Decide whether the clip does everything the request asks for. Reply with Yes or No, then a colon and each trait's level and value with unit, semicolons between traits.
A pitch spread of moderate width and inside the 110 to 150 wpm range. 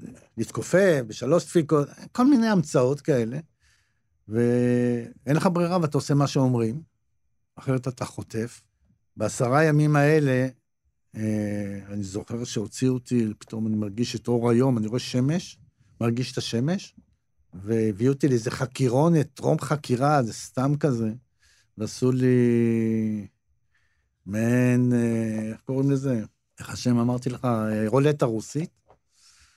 Yes: average, 4.1 semitones; average, 120 wpm